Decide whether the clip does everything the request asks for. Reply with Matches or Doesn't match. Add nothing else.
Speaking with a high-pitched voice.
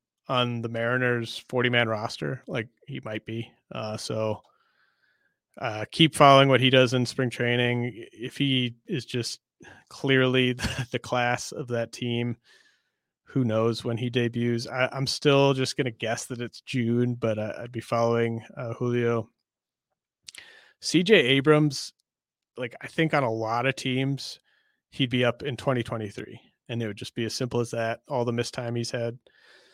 Doesn't match